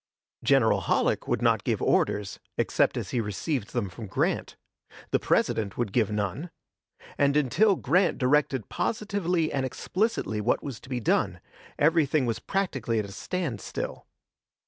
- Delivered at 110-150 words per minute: Yes, average, 145 wpm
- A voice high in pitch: No, low, 130 Hz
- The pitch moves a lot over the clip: Yes, wide, 7.3 semitones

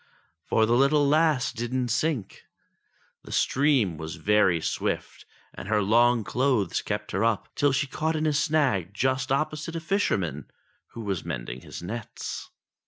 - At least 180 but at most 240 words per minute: No, average, 155 wpm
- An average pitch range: No, wide, 6.7 semitones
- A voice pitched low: Yes, low, 120 Hz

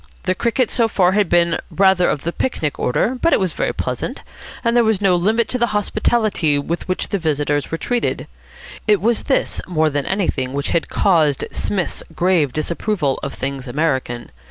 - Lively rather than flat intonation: Yes, wide, 6.1 semitones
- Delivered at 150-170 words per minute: No, average, 185 wpm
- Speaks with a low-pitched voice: No, medium, 180 Hz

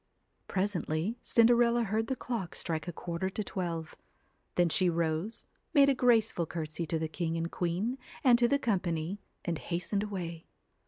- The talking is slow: No, average, 170 wpm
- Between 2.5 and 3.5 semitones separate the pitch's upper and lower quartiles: No, average, 5.3 semitones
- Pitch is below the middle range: No, medium, 185 Hz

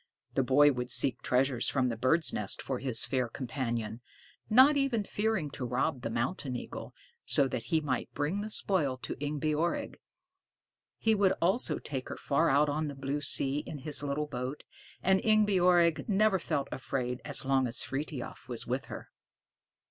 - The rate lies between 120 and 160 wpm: No, average, 170 wpm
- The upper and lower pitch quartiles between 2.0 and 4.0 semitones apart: No, average, 4.9 semitones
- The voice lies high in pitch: No, medium, 140 Hz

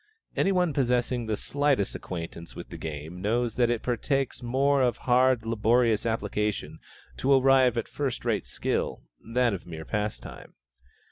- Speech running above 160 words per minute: No, average, 150 wpm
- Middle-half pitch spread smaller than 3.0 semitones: No, average, 3.6 semitones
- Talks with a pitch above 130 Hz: No, low, 120 Hz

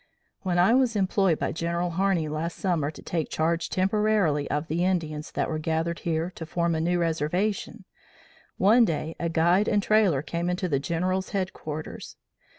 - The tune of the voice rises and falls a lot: No, average, 2.9 semitones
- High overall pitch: No, medium, 170 Hz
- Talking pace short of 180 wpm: Yes, average, 170 wpm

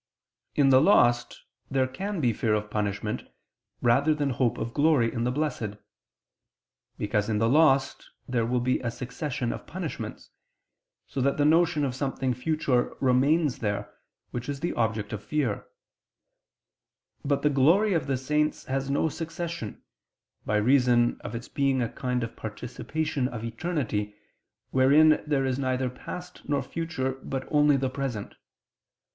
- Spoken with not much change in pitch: No, average, 3.8 semitones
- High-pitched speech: No, low, 130 Hz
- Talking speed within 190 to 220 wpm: No, average, 150 wpm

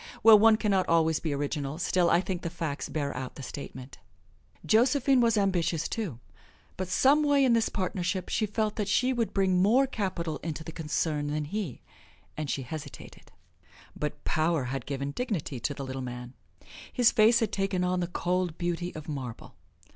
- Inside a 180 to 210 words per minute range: Yes, average, 185 wpm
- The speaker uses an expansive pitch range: Yes, wide, 6.3 semitones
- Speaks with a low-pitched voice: No, medium, 175 Hz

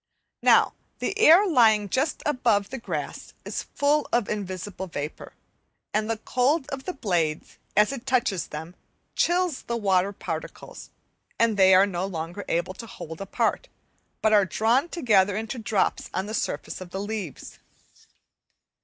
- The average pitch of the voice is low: No, high, 210 Hz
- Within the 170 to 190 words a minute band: No, average, 155 wpm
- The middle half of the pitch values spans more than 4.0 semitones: Yes, average, 5.2 semitones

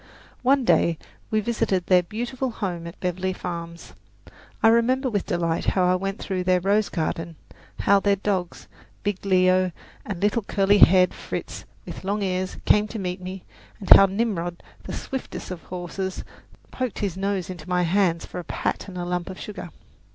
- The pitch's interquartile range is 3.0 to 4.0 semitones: No, narrow, 2.4 semitones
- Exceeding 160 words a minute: Yes, average, 180 wpm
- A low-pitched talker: No, high, 190 Hz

